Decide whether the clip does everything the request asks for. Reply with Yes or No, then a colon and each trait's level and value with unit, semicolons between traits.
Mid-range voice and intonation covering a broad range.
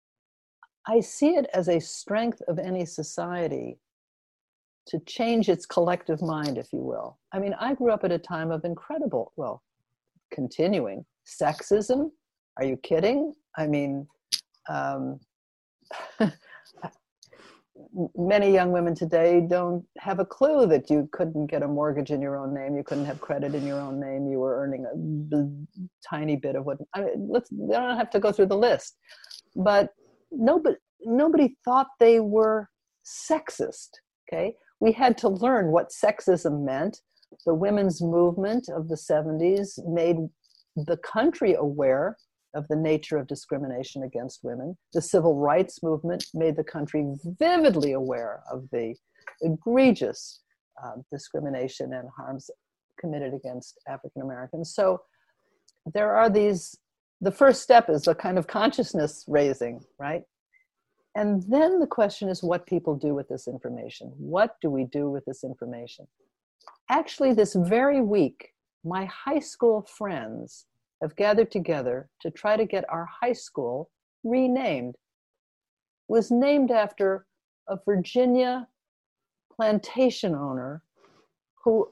Yes: medium, 175 Hz; wide, 7.4 semitones